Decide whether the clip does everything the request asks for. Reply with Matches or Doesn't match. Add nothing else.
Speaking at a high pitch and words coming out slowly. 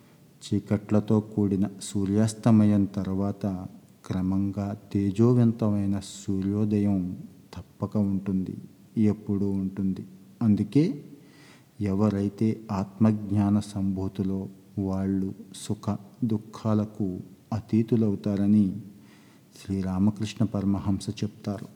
Doesn't match